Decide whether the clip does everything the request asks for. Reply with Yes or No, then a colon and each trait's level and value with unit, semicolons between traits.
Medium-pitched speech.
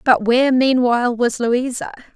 No: high, 245 Hz